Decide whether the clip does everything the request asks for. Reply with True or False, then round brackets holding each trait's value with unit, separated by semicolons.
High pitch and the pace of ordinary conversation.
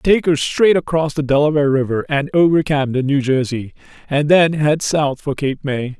False (145 Hz; 190 wpm)